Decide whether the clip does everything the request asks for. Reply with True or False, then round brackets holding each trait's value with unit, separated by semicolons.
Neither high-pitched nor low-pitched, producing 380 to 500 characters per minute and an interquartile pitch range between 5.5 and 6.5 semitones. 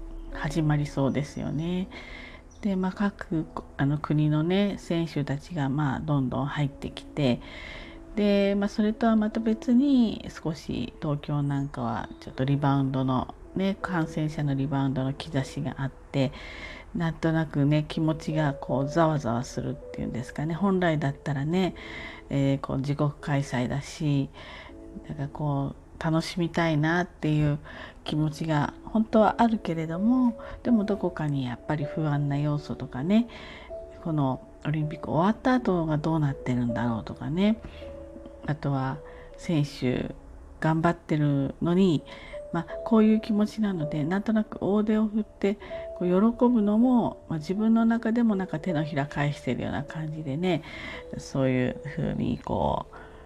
False (155 Hz; 305 characters per minute; 5.8 semitones)